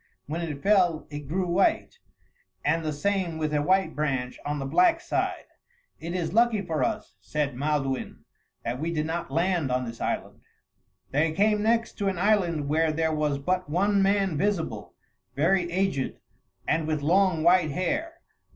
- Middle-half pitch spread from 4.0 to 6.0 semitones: Yes, average, 4.5 semitones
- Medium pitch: Yes, medium, 165 Hz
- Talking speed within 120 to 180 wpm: Yes, average, 170 wpm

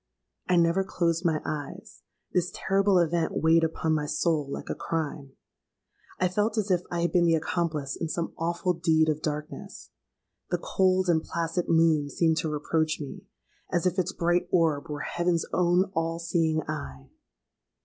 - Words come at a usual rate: Yes, average, 165 wpm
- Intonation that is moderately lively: No, narrow, 2.1 semitones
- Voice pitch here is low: No, medium, 165 Hz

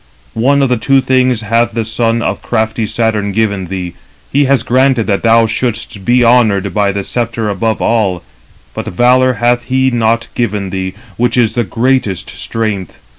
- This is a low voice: Yes, low, 115 Hz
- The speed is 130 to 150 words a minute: No, average, 170 wpm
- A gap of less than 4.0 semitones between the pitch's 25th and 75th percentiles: Yes, average, 2.9 semitones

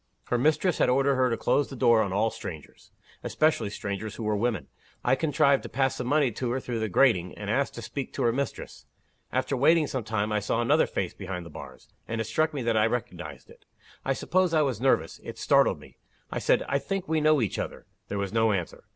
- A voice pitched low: Yes, low, 120 Hz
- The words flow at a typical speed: No, fast, 235 wpm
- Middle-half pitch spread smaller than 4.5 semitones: No, average, 4.9 semitones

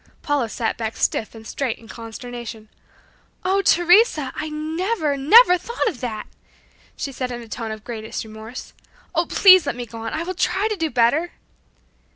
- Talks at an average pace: Yes, average, 180 wpm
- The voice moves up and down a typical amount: No, wide, 7.2 semitones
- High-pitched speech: Yes, very high, 260 Hz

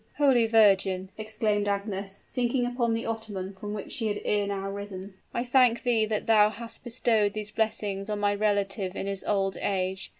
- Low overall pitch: No, high, 210 Hz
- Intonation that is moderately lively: No, narrow, 2.3 semitones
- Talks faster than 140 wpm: Yes, average, 180 wpm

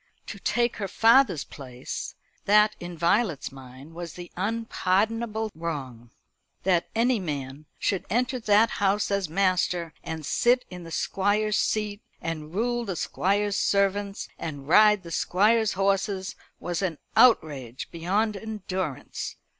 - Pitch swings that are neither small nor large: Yes, average, 4.5 semitones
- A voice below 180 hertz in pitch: No, high, 195 Hz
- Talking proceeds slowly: Yes, slow, 130 wpm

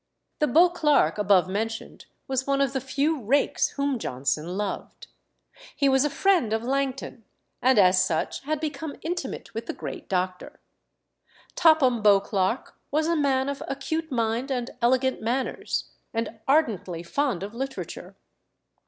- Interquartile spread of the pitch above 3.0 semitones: Yes, average, 5.0 semitones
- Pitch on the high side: Yes, very high, 260 Hz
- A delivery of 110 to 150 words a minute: Yes, average, 145 wpm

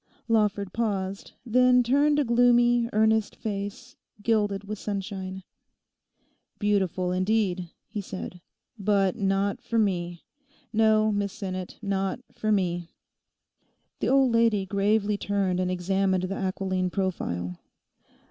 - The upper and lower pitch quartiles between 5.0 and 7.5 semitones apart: No, average, 2.7 semitones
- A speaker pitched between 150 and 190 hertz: No, high, 200 Hz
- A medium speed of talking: No, slow, 115 wpm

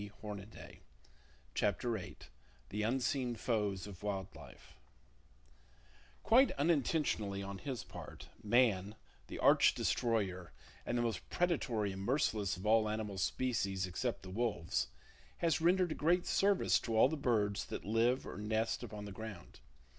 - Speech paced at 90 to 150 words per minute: Yes, average, 140 wpm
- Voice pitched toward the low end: Yes, low, 110 Hz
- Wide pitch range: No, average, 4.3 semitones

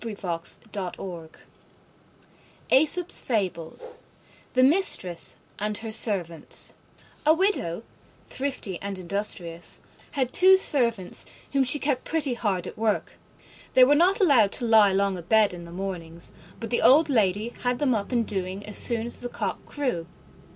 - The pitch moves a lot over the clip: Yes, wide, 6.1 semitones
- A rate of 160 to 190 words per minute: No, average, 150 wpm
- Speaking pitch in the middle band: No, high, 220 Hz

